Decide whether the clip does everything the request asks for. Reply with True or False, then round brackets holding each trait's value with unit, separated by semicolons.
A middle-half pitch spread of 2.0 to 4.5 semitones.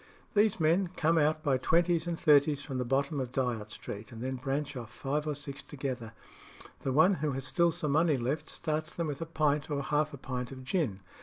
True (3.3 semitones)